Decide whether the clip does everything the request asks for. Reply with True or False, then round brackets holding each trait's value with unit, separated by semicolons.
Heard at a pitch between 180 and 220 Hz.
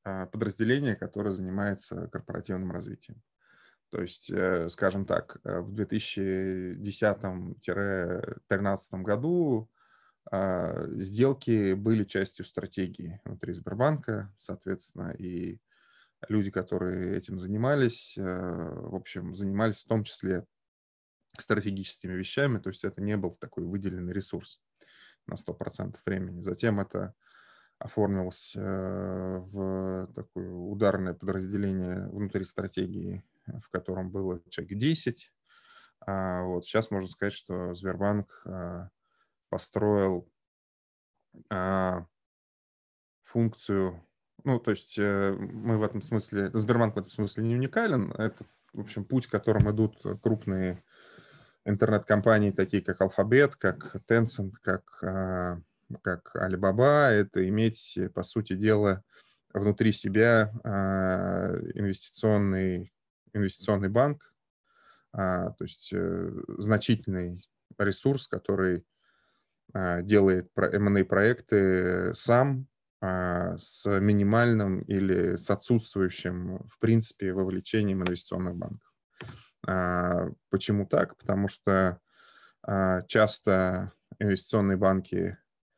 False (95 Hz)